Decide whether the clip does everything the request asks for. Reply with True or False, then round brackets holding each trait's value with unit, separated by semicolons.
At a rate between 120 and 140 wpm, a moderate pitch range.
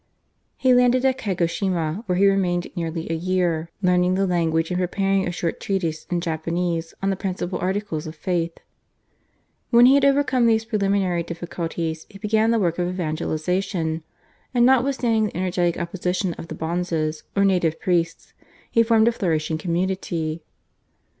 False (155 wpm; 3.1 semitones)